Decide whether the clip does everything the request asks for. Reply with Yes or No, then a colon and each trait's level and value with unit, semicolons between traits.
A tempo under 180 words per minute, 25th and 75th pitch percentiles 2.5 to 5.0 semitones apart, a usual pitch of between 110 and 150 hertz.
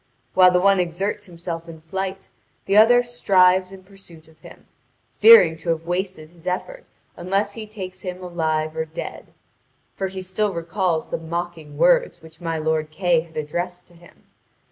No: average, 170 wpm; average, 2.9 semitones; medium, 180 Hz